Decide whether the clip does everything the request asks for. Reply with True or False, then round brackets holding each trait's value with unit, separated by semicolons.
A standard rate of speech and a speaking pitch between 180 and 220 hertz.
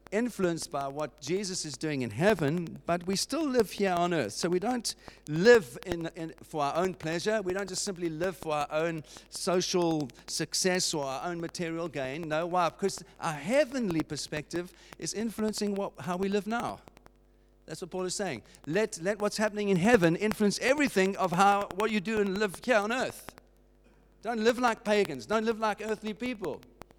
True (190 wpm; 185 Hz)